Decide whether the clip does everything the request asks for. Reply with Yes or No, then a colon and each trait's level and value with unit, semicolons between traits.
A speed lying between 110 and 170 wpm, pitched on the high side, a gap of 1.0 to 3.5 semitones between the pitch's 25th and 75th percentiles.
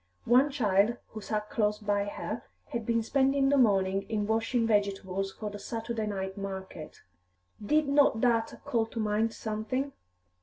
Yes: average, 155 wpm; high, 220 Hz; average, 2.8 semitones